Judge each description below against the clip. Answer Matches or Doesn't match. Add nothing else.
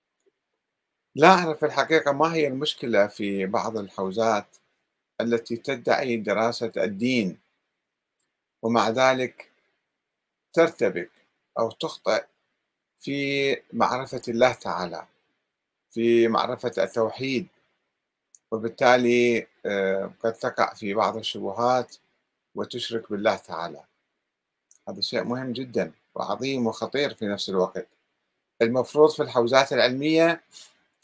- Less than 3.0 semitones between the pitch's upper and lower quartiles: Doesn't match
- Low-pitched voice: Matches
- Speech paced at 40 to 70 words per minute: Doesn't match